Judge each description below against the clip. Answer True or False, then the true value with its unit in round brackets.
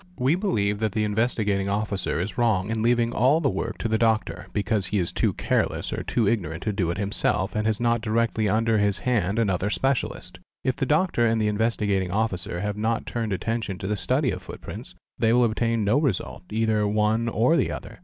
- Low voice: True (110 Hz)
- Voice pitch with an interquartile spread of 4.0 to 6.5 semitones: False (2.4 semitones)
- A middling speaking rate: False (210 wpm)